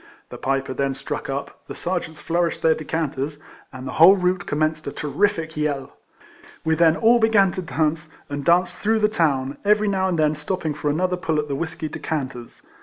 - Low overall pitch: No, medium, 160 Hz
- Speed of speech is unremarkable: No, fast, 210 wpm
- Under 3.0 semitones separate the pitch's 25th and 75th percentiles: No, average, 3.7 semitones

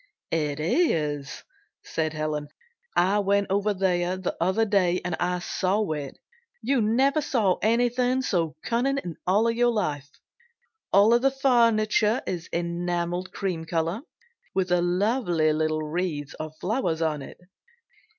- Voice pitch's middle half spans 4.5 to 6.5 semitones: Yes, wide, 5.6 semitones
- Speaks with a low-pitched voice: No, medium, 185 Hz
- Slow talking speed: Yes, slow, 125 wpm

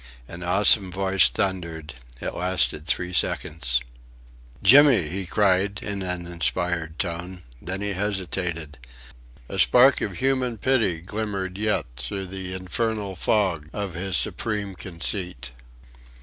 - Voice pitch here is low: Yes, very low, 95 Hz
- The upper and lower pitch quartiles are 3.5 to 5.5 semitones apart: No, average, 2.9 semitones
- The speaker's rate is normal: No, slow, 120 wpm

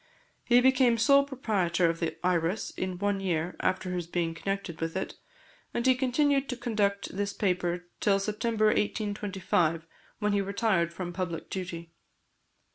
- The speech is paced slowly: No, average, 150 wpm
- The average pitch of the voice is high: Yes, high, 195 Hz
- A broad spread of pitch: No, average, 4.1 semitones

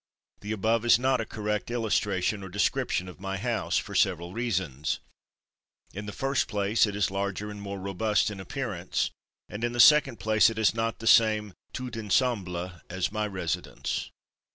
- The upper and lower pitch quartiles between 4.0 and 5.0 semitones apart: No, average, 2.9 semitones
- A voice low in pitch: Yes, low, 105 Hz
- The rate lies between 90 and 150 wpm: No, average, 175 wpm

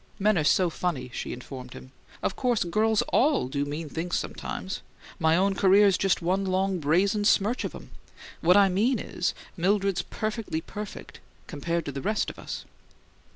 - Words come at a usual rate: Yes, average, 170 wpm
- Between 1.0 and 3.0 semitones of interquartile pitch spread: No, average, 4.0 semitones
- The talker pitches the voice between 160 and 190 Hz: Yes, medium, 185 Hz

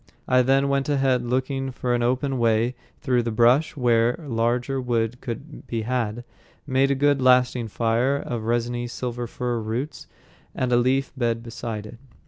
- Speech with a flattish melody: Yes, narrow, 2.1 semitones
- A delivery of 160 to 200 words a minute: Yes, average, 170 wpm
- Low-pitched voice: Yes, low, 125 Hz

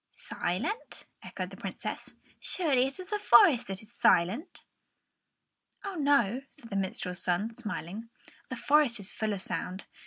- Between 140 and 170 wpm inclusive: Yes, average, 150 wpm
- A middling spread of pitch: No, wide, 6.9 semitones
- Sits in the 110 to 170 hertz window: No, high, 230 Hz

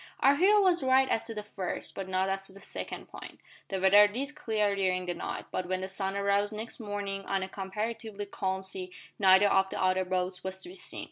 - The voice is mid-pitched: No, high, 195 Hz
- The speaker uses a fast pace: Yes, fast, 230 wpm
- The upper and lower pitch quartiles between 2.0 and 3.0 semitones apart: Yes, narrow, 2.4 semitones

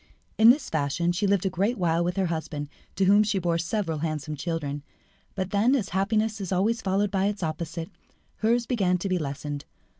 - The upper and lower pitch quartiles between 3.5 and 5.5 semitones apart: Yes, average, 3.9 semitones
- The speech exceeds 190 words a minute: Yes, average, 200 wpm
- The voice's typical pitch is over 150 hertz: Yes, medium, 185 Hz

